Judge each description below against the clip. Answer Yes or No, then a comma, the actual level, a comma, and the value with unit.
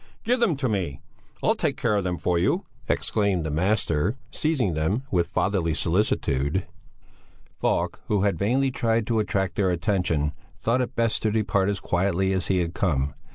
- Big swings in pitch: No, average, 4.2 semitones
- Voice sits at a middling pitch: No, very low, 95 Hz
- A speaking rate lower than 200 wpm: Yes, average, 175 wpm